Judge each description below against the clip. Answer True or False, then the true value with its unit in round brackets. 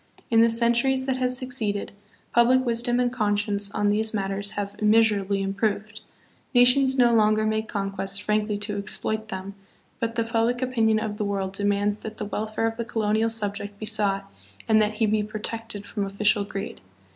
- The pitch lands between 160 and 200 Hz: False (215 Hz)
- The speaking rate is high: False (180 wpm)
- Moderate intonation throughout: False (2.1 semitones)